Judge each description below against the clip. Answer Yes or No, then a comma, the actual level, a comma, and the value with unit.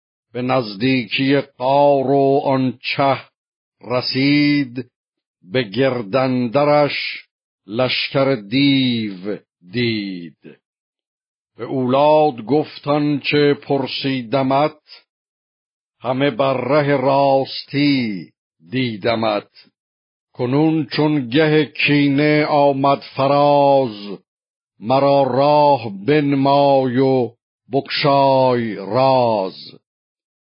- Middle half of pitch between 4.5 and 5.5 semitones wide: No, narrow, 2.5 semitones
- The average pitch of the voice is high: No, low, 135 Hz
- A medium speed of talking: No, slow, 65 wpm